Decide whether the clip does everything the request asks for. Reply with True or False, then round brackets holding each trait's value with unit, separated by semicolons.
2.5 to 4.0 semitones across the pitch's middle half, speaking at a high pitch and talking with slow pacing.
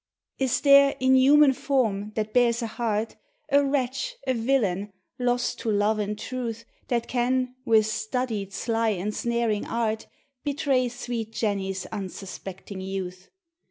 True (3.5 semitones; 230 Hz; 130 wpm)